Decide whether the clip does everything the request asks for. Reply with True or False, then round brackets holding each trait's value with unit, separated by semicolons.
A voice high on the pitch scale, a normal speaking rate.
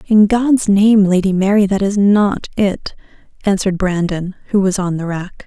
True (195 Hz; 175 wpm)